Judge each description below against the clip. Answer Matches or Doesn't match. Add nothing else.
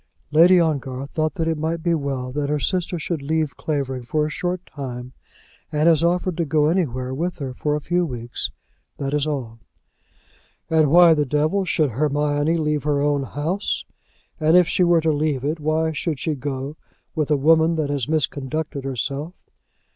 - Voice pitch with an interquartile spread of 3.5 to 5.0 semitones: Doesn't match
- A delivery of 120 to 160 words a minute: Doesn't match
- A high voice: Doesn't match